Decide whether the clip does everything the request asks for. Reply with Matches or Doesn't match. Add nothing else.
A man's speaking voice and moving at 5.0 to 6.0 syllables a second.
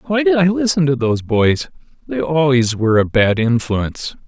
Matches